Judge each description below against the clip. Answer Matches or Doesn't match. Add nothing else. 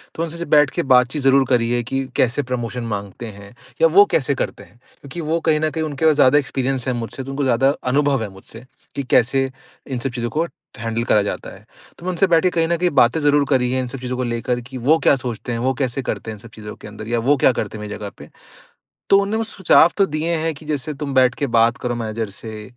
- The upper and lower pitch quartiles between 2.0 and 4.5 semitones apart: Matches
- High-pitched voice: Doesn't match